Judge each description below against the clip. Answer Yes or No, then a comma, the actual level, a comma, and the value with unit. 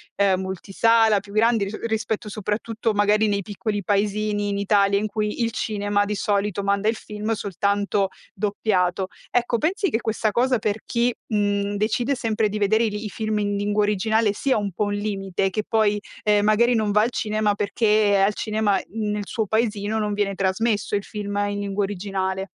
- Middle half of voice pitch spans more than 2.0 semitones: No, narrow, 1.3 semitones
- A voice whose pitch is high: Yes, high, 210 Hz